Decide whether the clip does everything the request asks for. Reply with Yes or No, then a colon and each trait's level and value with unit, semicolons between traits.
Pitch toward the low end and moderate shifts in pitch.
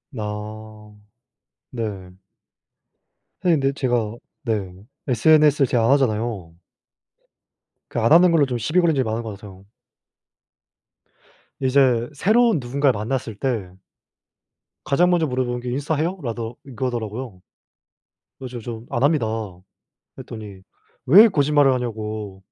Yes: low, 120 Hz; average, 4.5 semitones